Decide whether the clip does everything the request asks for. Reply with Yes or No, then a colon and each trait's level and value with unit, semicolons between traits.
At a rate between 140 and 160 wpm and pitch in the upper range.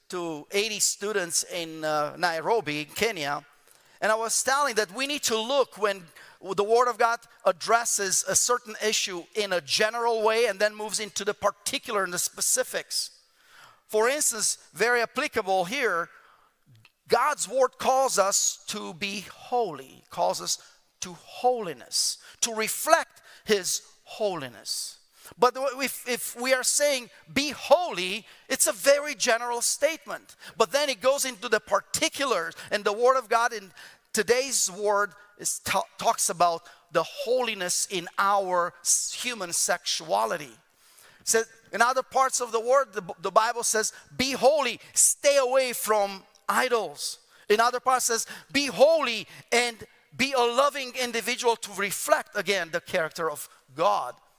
Yes: average, 150 wpm; high, 225 Hz